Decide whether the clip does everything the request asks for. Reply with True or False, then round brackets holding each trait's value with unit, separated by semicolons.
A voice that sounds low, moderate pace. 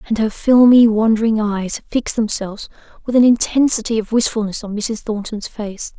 False (220 Hz; 160 wpm)